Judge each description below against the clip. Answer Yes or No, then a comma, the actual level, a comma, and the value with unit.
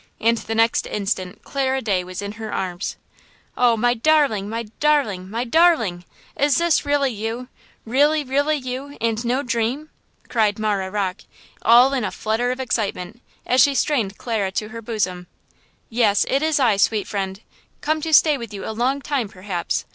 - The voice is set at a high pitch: Yes, high, 230 Hz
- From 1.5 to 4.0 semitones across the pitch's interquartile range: No, average, 4.9 semitones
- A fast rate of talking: No, average, 175 wpm